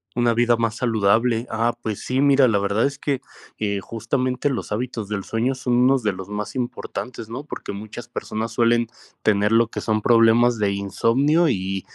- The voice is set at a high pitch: No, low, 115 Hz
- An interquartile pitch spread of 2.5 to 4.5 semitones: Yes, average, 2.8 semitones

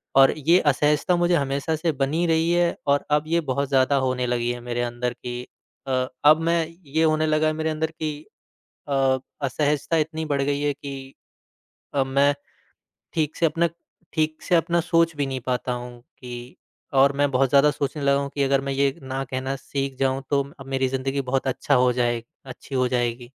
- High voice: No, medium, 140 Hz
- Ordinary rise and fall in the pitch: Yes, average, 3.0 semitones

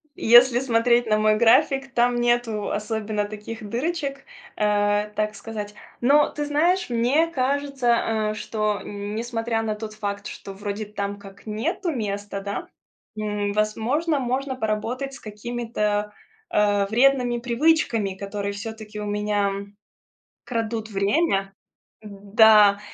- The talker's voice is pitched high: Yes, high, 220 Hz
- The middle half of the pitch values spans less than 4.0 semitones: Yes, average, 3.0 semitones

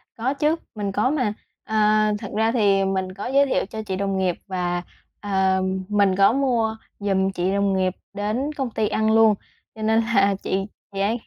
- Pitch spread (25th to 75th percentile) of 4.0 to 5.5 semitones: No, average, 2.7 semitones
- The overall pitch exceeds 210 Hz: No, high, 205 Hz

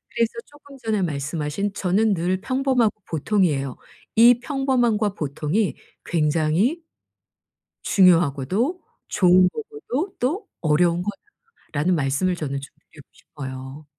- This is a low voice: No, medium, 185 Hz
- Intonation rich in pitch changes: Yes, wide, 7.6 semitones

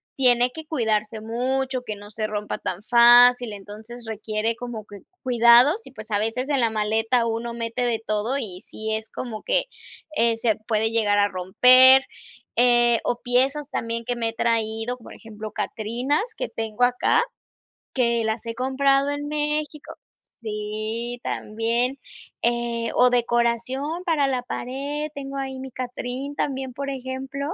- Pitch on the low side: No, high, 240 Hz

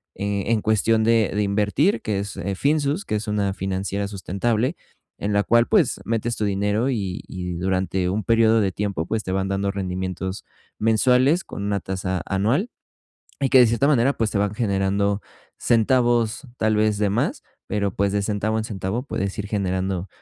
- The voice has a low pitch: Yes, low, 105 Hz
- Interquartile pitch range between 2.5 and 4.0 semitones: Yes, average, 2.8 semitones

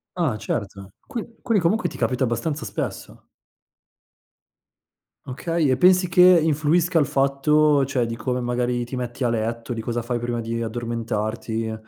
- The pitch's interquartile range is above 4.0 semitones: Yes, average, 4.7 semitones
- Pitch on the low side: Yes, low, 125 Hz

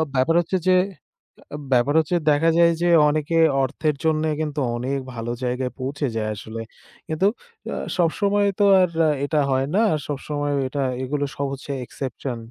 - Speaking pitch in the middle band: Yes, medium, 145 Hz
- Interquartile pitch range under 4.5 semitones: Yes, average, 3.5 semitones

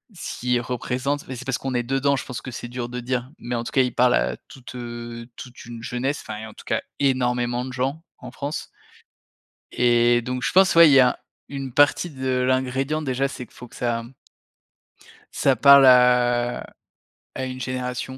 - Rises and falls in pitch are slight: Yes, narrow, 1.7 semitones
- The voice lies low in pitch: Yes, low, 125 Hz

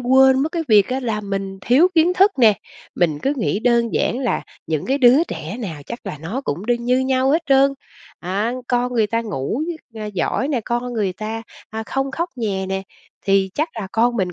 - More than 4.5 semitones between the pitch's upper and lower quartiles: Yes, average, 5.0 semitones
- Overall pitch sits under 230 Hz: No, high, 235 Hz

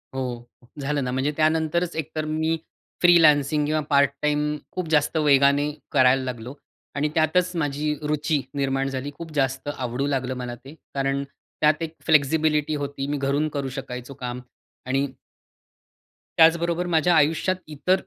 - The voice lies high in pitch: No, medium, 145 Hz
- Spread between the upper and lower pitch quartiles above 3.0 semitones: No, narrow, 2.6 semitones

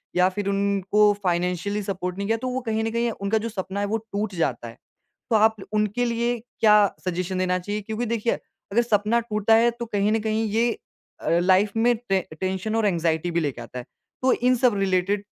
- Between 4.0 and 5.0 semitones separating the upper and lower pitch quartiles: No, average, 3.2 semitones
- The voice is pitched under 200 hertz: No, high, 205 Hz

